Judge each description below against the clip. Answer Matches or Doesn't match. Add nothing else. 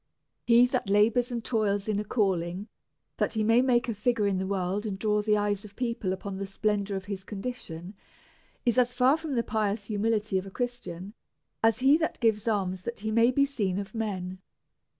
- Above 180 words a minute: Matches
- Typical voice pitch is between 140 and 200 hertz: Doesn't match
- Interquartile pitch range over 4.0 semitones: Doesn't match